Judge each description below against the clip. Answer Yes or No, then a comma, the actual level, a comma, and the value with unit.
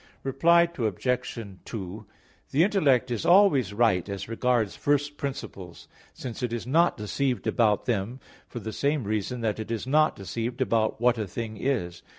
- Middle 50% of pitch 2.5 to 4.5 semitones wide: Yes, average, 4.2 semitones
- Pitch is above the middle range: No, low, 120 Hz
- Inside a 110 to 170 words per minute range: Yes, average, 160 wpm